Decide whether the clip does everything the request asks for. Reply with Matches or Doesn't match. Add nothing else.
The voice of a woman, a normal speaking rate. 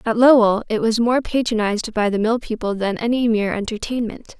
Matches